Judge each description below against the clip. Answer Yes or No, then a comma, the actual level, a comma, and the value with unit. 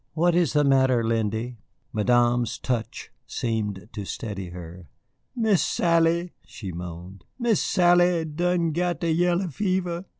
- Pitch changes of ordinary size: No, wide, 8.2 semitones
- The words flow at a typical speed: No, slow, 130 wpm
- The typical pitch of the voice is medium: Yes, medium, 145 Hz